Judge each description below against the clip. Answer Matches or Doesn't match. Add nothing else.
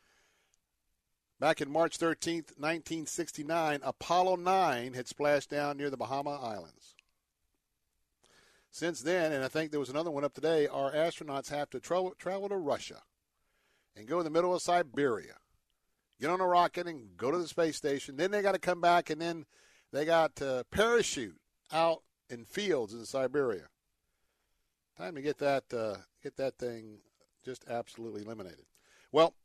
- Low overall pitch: Doesn't match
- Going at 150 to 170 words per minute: Matches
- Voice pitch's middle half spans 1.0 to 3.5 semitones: Doesn't match